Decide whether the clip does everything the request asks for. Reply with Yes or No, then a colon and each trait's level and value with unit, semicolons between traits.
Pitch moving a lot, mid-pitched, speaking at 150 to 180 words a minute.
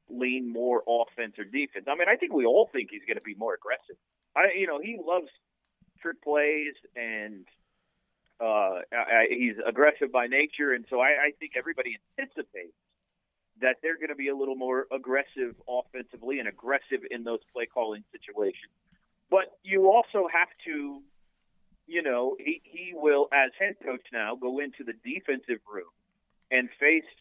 Yes: wide, 7.5 semitones; medium, 150 Hz; average, 170 wpm